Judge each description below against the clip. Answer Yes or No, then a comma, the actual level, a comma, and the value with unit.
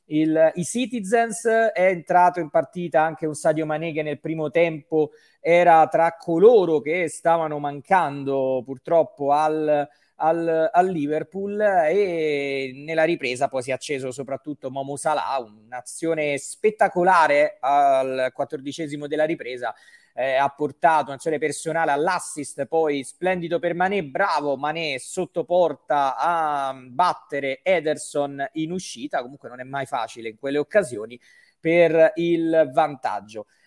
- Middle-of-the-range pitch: Yes, medium, 155 Hz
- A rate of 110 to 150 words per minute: Yes, average, 125 wpm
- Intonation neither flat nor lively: Yes, average, 3.5 semitones